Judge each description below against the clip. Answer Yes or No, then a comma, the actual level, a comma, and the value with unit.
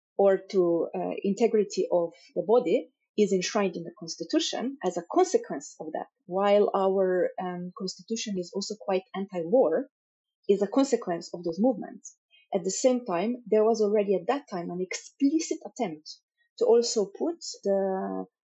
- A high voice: Yes, high, 200 Hz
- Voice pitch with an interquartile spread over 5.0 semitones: Yes, wide, 5.4 semitones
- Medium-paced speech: Yes, average, 155 wpm